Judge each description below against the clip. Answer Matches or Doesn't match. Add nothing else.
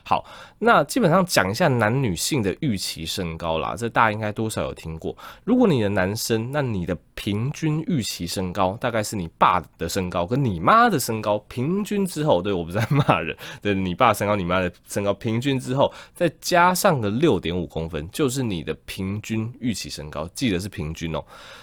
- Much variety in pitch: Matches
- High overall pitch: Doesn't match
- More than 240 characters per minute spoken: Matches